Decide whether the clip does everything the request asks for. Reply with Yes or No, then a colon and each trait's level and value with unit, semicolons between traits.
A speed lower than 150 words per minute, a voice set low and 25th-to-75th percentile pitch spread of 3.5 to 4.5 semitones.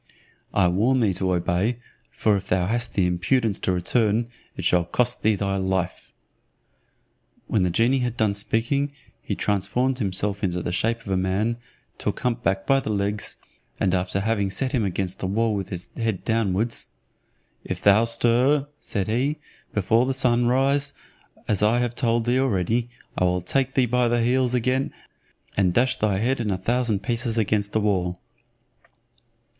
No: average, 175 wpm; low, 110 Hz; average, 4.1 semitones